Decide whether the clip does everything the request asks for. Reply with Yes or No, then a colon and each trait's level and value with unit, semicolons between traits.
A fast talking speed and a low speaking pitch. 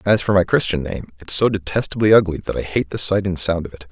Yes: fast, 275 wpm; very low, 95 Hz